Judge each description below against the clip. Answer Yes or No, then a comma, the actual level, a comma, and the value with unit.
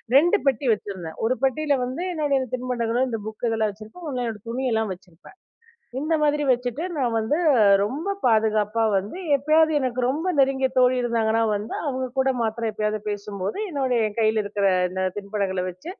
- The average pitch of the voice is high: Yes, high, 235 Hz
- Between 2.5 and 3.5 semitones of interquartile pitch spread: No, average, 4.0 semitones